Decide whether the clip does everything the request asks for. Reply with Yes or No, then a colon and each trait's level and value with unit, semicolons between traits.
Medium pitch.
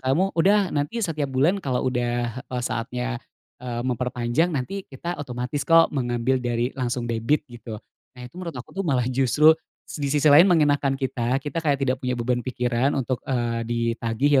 No: low, 130 Hz